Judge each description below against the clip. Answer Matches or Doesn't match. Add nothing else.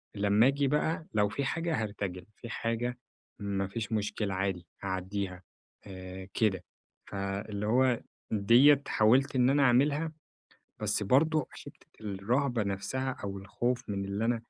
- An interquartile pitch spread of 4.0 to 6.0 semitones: Matches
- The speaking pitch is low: Matches